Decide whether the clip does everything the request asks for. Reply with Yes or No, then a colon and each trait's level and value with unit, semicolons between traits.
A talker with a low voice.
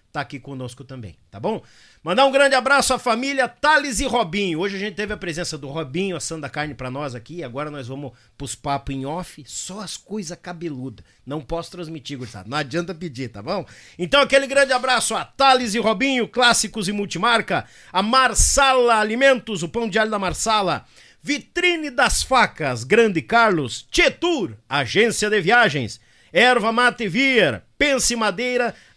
No: high, 205 Hz